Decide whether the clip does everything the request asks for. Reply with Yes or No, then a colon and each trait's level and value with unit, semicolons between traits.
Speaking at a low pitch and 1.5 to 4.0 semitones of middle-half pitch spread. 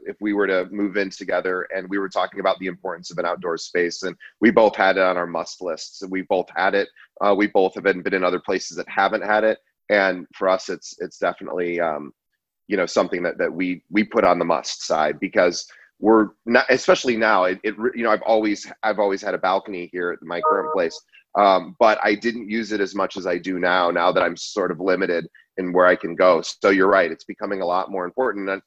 Yes: very low, 95 Hz; average, 2.9 semitones